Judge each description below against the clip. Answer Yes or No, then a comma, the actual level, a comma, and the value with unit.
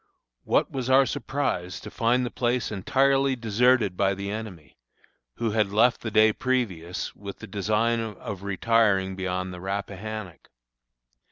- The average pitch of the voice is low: Yes, low, 110 Hz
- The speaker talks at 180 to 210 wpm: No, average, 145 wpm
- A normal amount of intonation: Yes, average, 3.8 semitones